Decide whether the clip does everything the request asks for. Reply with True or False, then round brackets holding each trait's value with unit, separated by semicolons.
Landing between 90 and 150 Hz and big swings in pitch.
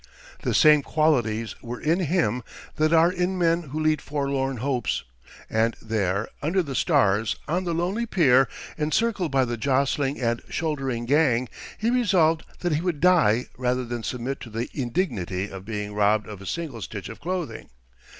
True (135 Hz; 6.2 semitones)